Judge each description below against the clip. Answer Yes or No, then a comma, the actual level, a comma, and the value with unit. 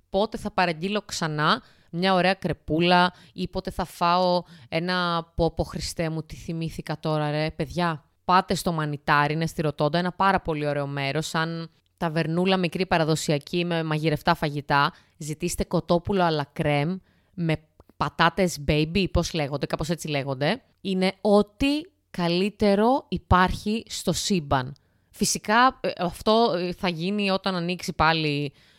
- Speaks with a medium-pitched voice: Yes, medium, 175 Hz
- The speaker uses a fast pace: No, average, 130 wpm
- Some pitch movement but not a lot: Yes, average, 3.2 semitones